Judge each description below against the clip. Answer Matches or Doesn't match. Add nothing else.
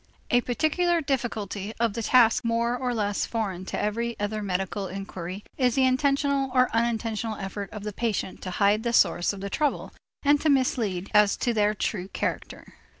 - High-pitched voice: Matches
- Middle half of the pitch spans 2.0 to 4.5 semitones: Matches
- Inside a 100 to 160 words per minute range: Doesn't match